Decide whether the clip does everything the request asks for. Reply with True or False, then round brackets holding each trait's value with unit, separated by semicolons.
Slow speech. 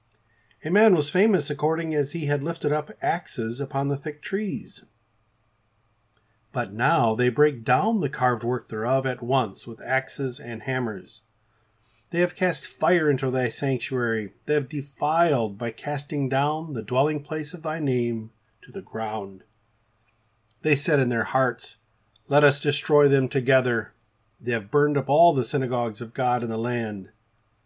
False (160 wpm)